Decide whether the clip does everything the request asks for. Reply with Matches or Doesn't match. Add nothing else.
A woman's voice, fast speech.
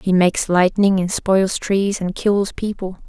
Doesn't match